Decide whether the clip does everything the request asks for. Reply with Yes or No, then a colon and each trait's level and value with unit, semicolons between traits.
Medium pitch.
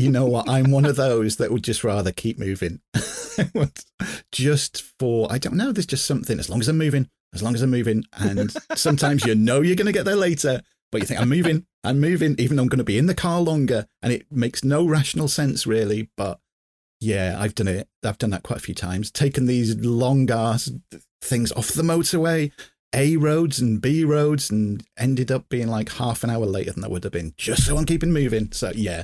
No: low, 125 Hz